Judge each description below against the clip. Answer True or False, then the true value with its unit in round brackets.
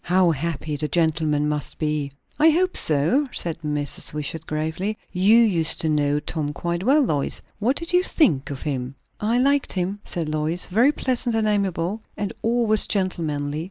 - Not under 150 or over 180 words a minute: True (170 wpm)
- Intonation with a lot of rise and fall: True (6.4 semitones)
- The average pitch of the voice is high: False (170 Hz)